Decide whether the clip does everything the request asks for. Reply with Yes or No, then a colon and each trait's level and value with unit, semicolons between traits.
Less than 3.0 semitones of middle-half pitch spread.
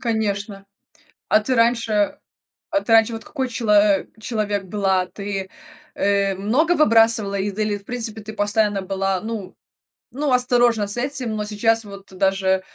Yes: narrow, 2.5 semitones